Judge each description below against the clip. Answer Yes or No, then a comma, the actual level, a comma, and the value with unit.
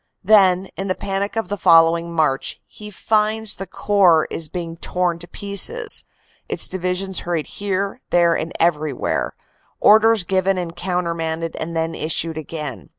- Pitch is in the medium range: Yes, medium, 180 Hz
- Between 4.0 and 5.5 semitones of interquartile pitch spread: No, average, 3.2 semitones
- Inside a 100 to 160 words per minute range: Yes, average, 150 wpm